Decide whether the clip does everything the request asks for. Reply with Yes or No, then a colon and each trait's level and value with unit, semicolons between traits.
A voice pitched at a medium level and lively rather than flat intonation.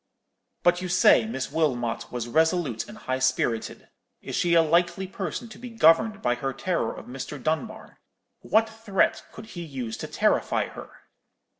Yes: medium, 165 Hz; wide, 6.8 semitones